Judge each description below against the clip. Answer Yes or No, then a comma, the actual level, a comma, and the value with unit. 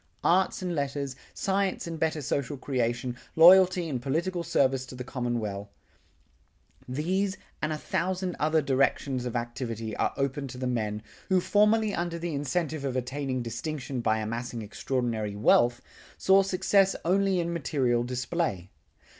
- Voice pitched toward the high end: No, medium, 140 Hz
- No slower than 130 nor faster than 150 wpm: Yes, average, 145 wpm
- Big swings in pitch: Yes, wide, 6.0 semitones